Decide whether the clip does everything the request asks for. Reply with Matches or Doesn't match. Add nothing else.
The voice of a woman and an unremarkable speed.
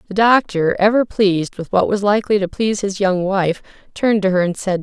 Doesn't match